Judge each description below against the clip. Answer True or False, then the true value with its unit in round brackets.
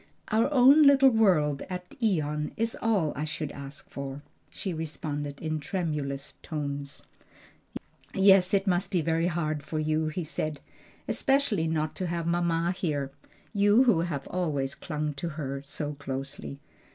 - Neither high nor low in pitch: True (160 Hz)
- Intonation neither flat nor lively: True (4.0 semitones)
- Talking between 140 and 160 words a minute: True (150 wpm)